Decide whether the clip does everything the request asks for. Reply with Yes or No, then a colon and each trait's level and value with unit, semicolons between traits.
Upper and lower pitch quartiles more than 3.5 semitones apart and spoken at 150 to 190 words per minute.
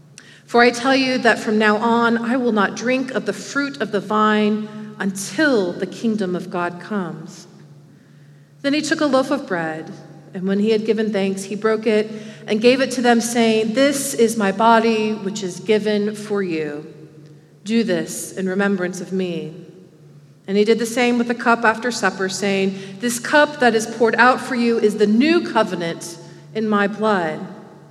Yes: average, 4.0 semitones; average, 185 wpm